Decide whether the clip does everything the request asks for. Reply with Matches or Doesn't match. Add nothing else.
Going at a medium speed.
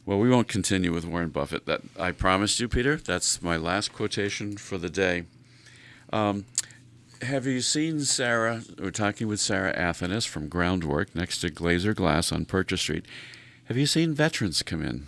Matches